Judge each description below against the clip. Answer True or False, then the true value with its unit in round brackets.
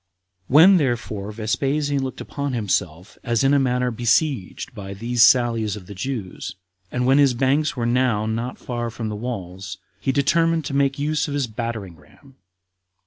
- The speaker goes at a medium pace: True (175 wpm)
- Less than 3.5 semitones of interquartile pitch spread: False (4.2 semitones)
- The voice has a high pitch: False (120 Hz)